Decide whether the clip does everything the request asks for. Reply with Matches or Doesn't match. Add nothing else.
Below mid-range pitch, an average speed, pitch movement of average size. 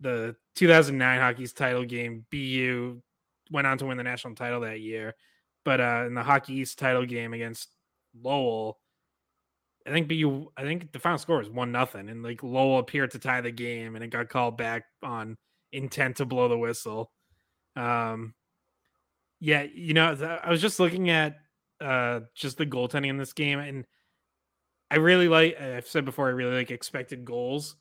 Matches